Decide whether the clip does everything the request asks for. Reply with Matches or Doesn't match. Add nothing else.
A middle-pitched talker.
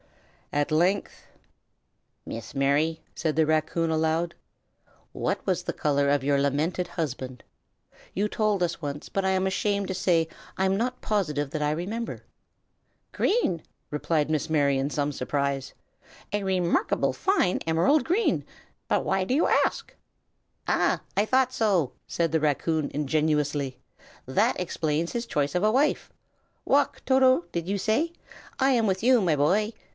Matches